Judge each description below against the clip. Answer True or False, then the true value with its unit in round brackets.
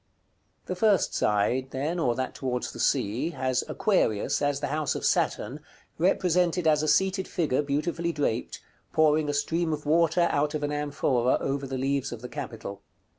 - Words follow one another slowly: False (180 wpm)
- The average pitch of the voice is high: False (145 Hz)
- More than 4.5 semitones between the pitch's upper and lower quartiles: False (4.0 semitones)